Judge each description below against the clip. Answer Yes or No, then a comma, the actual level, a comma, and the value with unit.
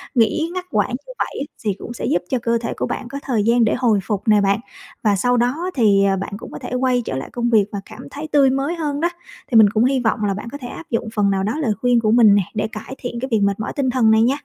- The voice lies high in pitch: Yes, high, 235 Hz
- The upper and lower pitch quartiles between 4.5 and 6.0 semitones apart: No, average, 3.7 semitones